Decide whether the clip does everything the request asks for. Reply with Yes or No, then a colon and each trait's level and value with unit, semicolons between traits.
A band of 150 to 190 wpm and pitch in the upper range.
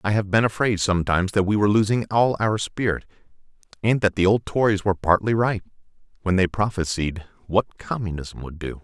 No: average, 185 wpm; low, 100 Hz